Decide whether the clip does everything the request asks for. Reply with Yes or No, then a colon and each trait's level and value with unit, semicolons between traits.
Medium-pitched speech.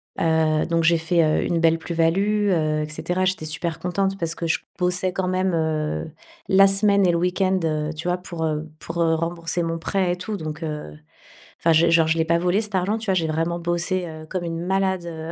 Yes: medium, 170 Hz